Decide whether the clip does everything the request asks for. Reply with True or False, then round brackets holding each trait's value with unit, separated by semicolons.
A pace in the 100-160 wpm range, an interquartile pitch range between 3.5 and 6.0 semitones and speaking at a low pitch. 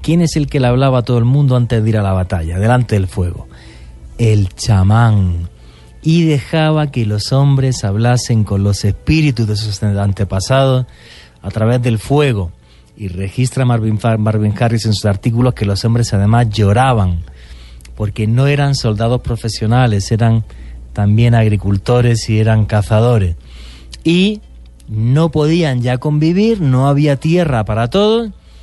True (150 wpm; 4.5 semitones; 115 Hz)